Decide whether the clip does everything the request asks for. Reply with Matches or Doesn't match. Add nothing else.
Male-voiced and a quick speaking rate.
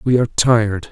Doesn't match